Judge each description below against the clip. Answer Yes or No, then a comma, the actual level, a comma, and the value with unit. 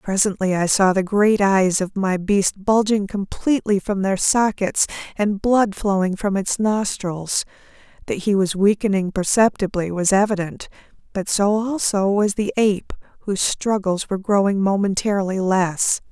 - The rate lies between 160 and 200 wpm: No, average, 145 wpm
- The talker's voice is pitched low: No, high, 200 Hz